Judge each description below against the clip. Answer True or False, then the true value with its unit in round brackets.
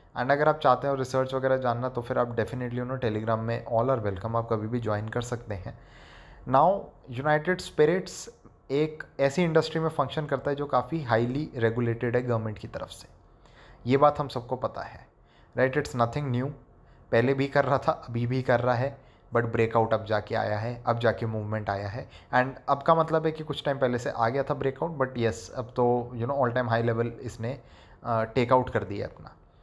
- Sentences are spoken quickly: True (210 wpm)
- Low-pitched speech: True (125 Hz)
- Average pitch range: True (3.3 semitones)